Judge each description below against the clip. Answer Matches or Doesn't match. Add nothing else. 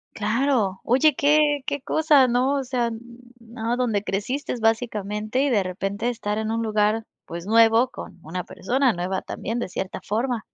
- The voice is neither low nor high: Doesn't match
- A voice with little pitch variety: Doesn't match